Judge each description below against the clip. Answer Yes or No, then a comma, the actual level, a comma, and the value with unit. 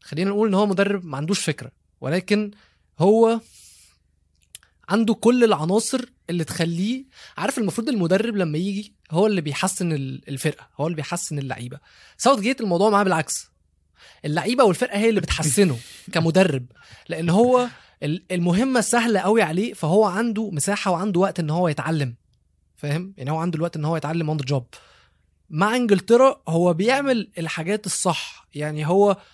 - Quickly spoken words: Yes, fast, 145 wpm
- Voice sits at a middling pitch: Yes, medium, 180 Hz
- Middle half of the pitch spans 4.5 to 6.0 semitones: Yes, wide, 5.6 semitones